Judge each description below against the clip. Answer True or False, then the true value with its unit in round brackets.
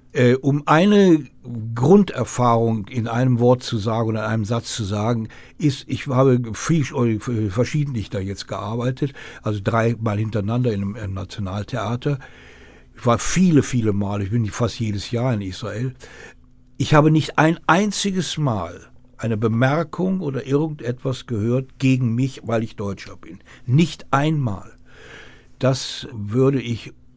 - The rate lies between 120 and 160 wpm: True (135 wpm)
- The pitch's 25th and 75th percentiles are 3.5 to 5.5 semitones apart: True (3.9 semitones)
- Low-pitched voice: True (120 Hz)